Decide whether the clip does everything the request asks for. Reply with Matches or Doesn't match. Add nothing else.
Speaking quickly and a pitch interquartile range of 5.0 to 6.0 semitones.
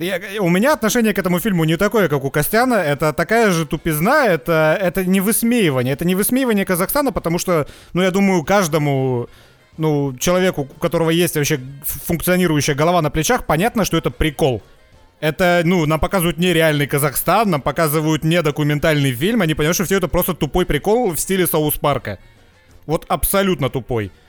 Doesn't match